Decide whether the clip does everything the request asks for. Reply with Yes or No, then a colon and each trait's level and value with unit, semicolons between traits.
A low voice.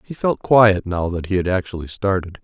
Yes: very low, 95 Hz